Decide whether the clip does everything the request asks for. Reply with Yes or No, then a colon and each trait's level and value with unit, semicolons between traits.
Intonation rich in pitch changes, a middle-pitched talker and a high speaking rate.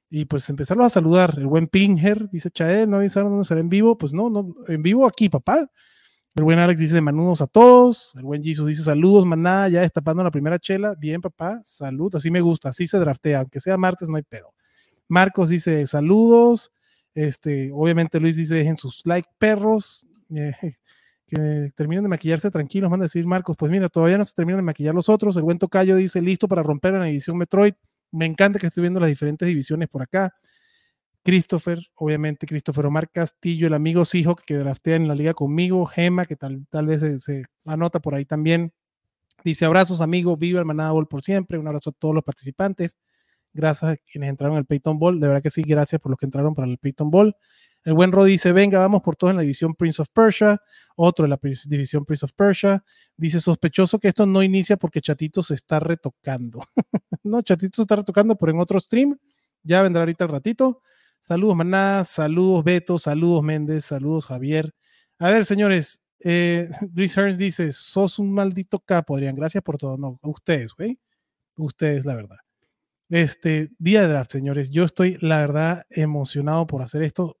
No: average, 3.9 semitones; medium, 170 Hz; fast, 200 wpm